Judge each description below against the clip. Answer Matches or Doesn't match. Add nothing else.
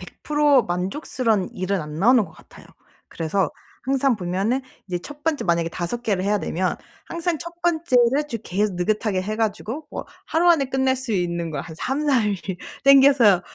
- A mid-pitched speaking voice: Doesn't match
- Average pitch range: Doesn't match